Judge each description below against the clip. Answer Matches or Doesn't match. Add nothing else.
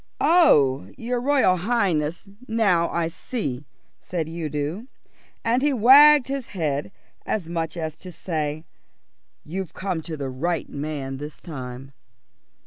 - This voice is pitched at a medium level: Matches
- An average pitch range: Doesn't match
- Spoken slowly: Matches